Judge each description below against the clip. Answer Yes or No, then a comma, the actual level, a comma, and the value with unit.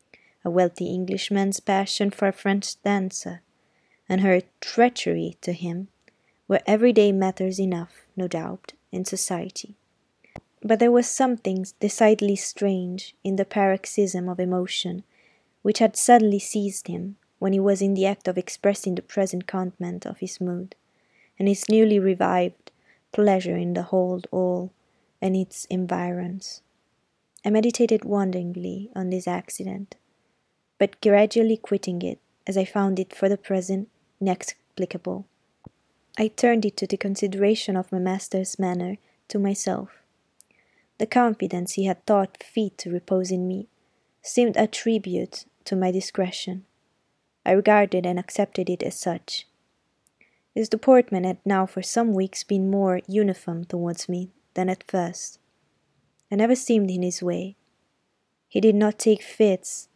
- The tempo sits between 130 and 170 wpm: Yes, average, 140 wpm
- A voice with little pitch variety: Yes, narrow, 2.2 semitones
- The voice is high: Yes, high, 195 Hz